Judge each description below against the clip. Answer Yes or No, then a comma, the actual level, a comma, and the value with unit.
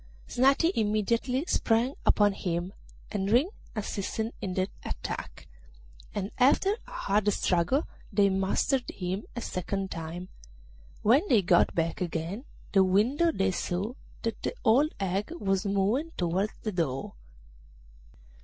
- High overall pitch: Yes, high, 200 Hz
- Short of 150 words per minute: Yes, slow, 135 wpm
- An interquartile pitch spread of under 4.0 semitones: No, average, 4.3 semitones